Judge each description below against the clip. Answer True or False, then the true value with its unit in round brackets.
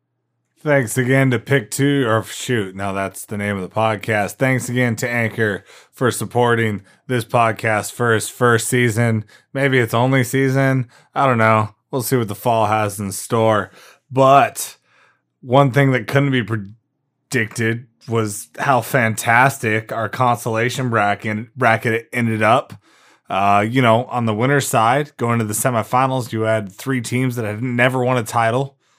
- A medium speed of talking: True (160 wpm)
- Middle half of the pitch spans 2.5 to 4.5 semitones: True (2.9 semitones)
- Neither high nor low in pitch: False (120 Hz)